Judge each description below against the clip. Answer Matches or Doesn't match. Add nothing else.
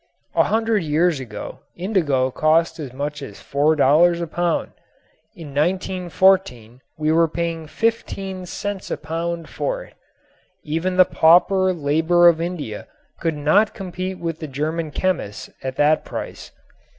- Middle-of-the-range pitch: Matches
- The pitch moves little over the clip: Doesn't match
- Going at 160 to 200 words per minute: Doesn't match